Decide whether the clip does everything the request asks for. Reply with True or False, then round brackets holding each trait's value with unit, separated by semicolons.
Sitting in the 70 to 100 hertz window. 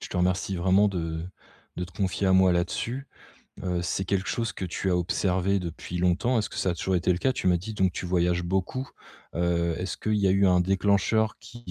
True (95 Hz)